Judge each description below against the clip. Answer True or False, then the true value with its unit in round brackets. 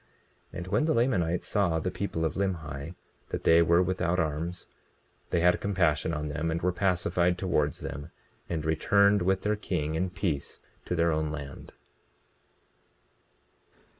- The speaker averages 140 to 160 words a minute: True (155 wpm)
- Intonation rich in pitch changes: False (2.8 semitones)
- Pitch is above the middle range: False (85 Hz)